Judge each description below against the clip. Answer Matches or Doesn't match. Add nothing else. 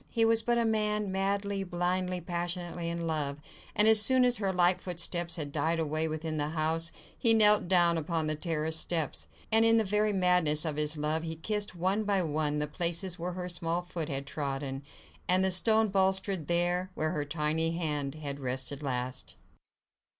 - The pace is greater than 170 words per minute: Matches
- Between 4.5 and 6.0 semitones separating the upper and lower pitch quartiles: Doesn't match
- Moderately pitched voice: Matches